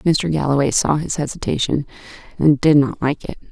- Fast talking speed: No, average, 170 wpm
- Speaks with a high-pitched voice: No, medium, 145 Hz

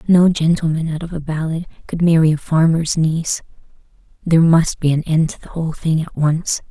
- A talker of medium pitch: Yes, medium, 160 Hz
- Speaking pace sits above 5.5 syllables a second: No, 5.4 syllables/s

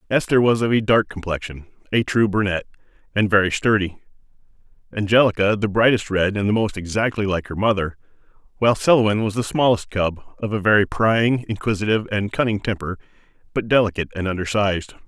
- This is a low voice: Yes, low, 105 Hz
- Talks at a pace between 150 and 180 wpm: Yes, average, 165 wpm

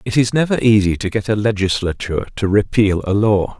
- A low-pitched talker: Yes, low, 105 Hz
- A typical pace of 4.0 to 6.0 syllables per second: Yes, 5.7 syllables/s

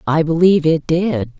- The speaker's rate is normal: Yes, average, 170 wpm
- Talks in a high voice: No, medium, 160 Hz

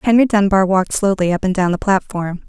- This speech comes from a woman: Yes, female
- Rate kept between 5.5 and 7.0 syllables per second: Yes, 6.0 syllables/s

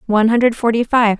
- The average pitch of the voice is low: No, high, 225 Hz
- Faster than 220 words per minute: No, average, 200 wpm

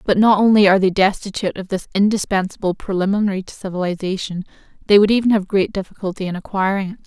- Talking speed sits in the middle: Yes, average, 180 wpm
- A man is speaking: No, female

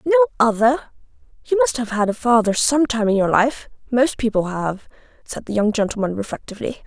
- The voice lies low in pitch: No, high, 240 Hz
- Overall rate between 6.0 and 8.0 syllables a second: No, 5.6 syllables/s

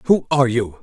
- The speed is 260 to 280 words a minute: No, fast, 215 wpm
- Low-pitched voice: Yes, low, 130 Hz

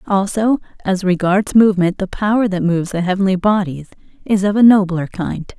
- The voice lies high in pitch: Yes, high, 195 Hz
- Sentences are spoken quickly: No, average, 170 wpm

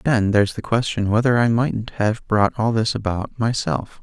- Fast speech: Yes, fast, 210 wpm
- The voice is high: No, low, 110 Hz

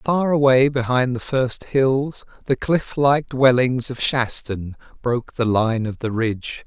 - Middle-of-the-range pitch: No, low, 125 Hz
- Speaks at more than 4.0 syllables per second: No, 3.9 syllables/s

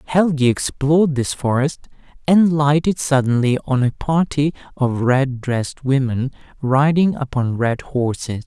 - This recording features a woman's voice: No, male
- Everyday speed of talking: No, slow, 130 wpm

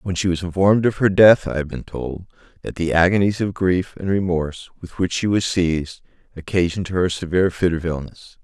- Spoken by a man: Yes, male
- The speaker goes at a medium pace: No, fast, 215 wpm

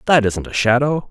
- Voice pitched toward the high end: No, low, 125 Hz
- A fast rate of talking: Yes, fast, 215 wpm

